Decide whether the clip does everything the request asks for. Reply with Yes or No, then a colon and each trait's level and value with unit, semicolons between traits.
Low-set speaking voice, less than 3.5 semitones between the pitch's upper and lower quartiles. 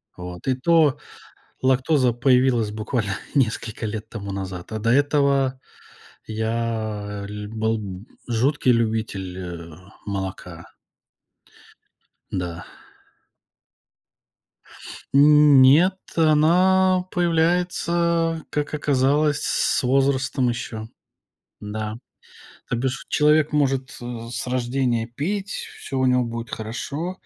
No: low, 125 Hz; average, 5.2 semitones